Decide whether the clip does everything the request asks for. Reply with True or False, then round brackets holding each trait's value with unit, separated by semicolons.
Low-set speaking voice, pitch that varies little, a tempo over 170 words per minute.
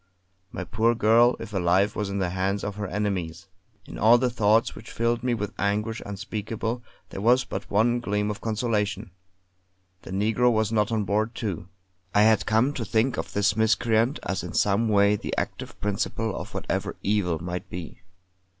True (105 Hz; 2.2 semitones; 180 wpm)